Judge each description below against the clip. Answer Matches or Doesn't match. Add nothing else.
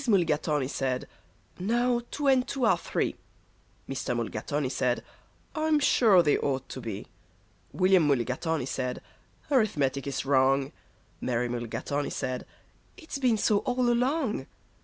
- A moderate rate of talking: Doesn't match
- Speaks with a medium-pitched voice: Matches